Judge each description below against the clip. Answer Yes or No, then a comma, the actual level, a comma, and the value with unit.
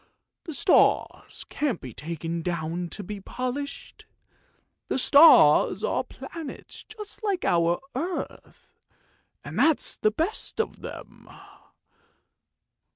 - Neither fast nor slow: No, slow, 110 wpm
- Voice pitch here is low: No, very high, 250 Hz